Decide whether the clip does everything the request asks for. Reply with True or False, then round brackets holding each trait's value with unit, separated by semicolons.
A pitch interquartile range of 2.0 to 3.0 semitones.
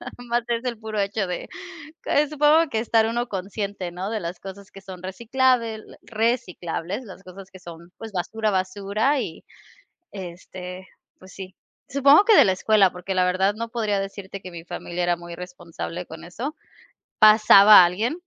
False (3.9 semitones)